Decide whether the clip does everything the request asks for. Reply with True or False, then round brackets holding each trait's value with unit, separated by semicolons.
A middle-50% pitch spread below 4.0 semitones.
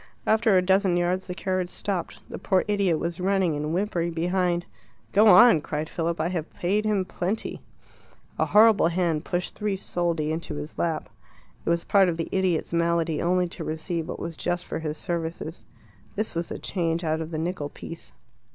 True (2.4 semitones)